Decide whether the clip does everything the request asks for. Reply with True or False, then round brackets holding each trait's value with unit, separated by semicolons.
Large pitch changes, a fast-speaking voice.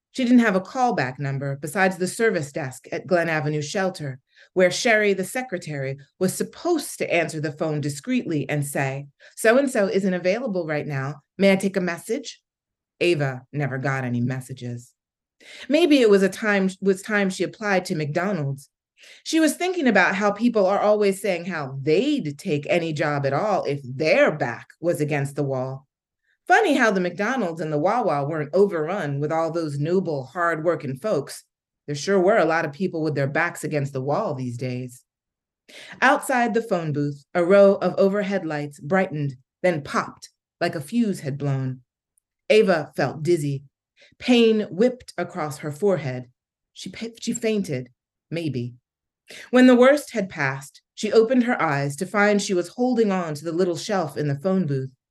False (5.9 semitones; 175 wpm)